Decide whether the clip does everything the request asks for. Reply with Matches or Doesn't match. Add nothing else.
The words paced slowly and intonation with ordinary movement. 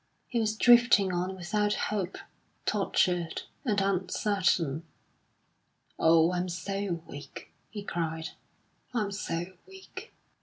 Matches